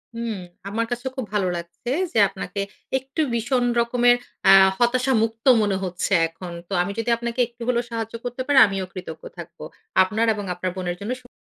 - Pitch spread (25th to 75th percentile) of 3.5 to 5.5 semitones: Yes, average, 4.5 semitones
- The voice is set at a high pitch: Yes, high, 225 Hz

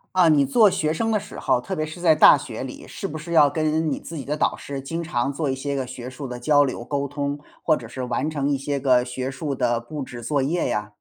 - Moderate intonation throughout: Yes, average, 3.2 semitones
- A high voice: No, medium, 140 Hz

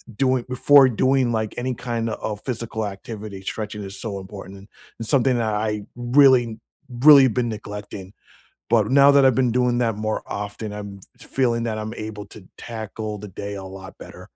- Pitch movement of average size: Yes, average, 3.2 semitones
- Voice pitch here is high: No, low, 110 Hz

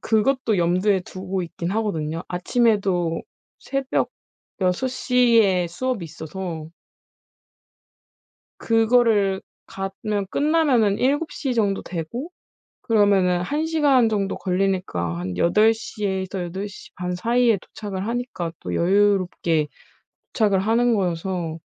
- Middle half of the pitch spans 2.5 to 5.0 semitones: Yes, average, 4.4 semitones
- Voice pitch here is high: Yes, high, 195 Hz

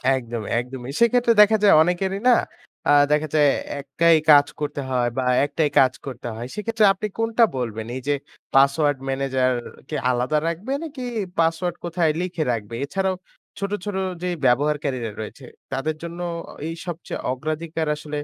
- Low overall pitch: No, medium, 150 Hz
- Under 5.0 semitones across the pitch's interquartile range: No, average, 5.3 semitones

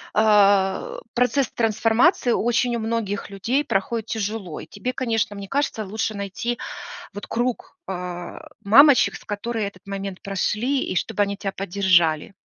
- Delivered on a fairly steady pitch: No, average, 3.4 semitones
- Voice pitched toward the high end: Yes, high, 215 Hz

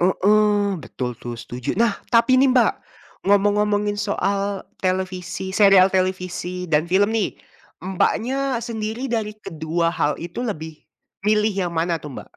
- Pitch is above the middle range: Yes, high, 195 Hz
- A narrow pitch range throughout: No, average, 3.3 semitones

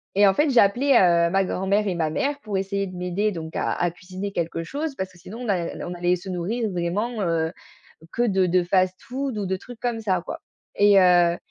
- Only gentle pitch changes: No, average, 3.3 semitones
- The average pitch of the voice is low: No, high, 190 Hz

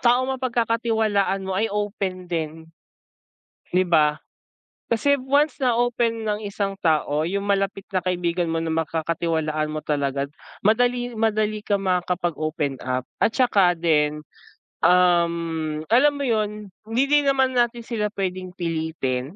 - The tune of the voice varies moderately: No, wide, 5.7 semitones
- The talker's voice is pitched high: Yes, high, 195 Hz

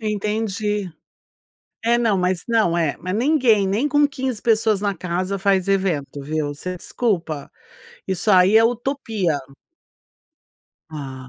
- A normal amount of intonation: Yes, average, 4.2 semitones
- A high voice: Yes, high, 200 Hz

